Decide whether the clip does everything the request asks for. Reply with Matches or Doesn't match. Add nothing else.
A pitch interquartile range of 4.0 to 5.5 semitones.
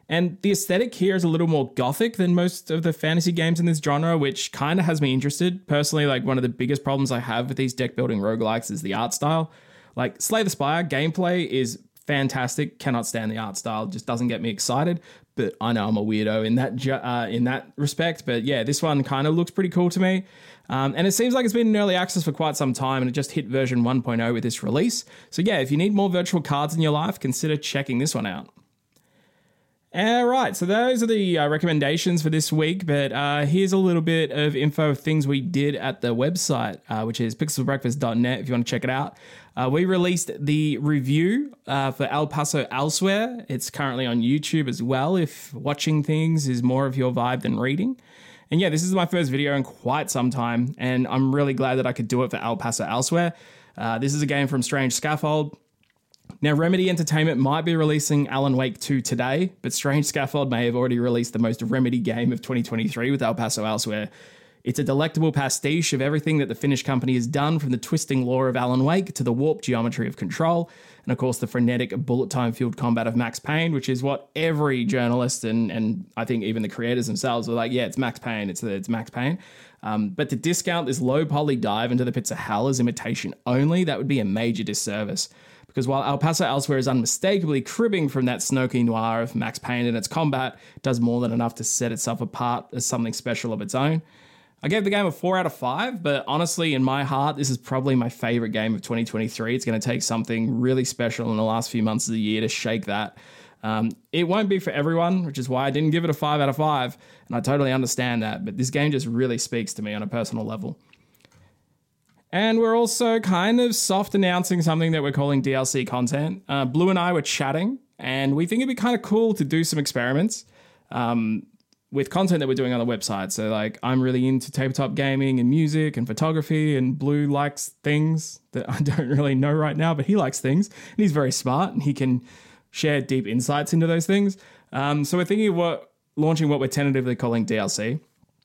Matches